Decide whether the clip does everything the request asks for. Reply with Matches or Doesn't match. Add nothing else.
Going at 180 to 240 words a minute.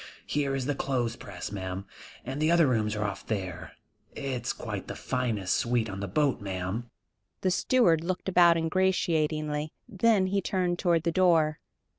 Doesn't match